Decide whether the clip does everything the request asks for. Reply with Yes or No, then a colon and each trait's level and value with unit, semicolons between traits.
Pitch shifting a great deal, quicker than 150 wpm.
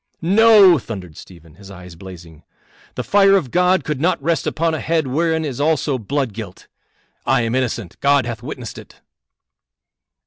Yes: wide, 8.1 semitones; average, 165 wpm